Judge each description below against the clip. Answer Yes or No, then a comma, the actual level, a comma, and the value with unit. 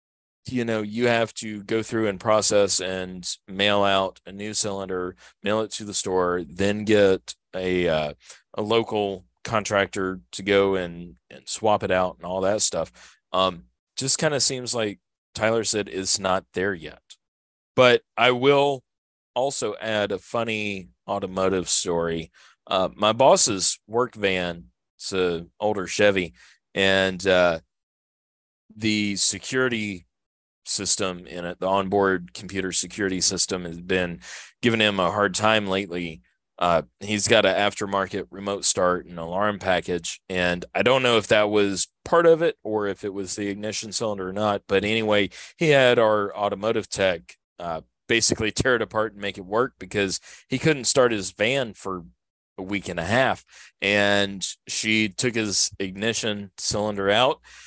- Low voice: Yes, low, 100 Hz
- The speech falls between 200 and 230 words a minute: No, average, 155 wpm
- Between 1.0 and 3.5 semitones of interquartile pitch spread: Yes, average, 2.8 semitones